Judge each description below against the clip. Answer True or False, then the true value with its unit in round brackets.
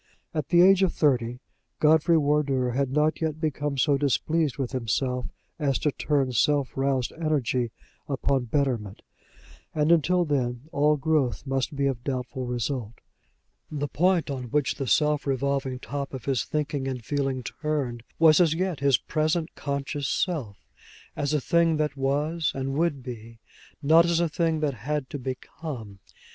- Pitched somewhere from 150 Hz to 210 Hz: False (140 Hz)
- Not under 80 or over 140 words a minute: False (160 wpm)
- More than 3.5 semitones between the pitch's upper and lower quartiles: False (3.0 semitones)